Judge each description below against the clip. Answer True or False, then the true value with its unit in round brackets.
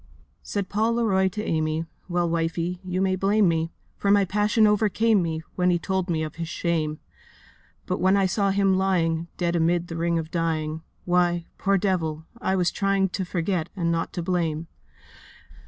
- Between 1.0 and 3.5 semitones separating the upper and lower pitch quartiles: True (2.7 semitones)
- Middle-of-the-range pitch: True (175 Hz)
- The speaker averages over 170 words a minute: True (180 wpm)